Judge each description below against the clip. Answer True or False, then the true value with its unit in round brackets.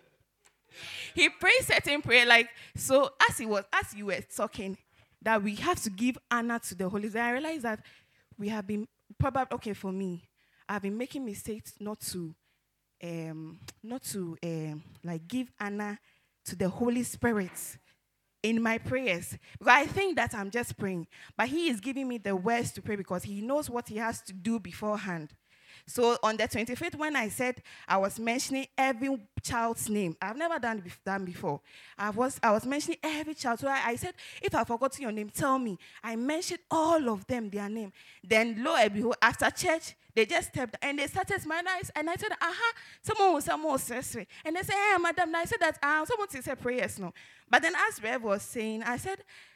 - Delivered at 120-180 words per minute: False (200 wpm)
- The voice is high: True (235 Hz)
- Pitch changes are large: True (5.9 semitones)